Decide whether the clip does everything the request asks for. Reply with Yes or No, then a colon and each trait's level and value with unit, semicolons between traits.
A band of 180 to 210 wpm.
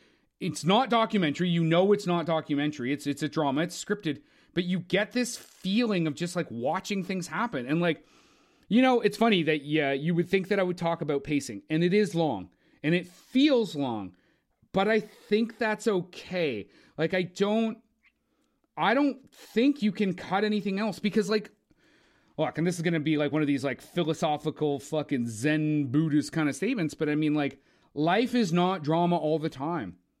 Yes: average, 195 wpm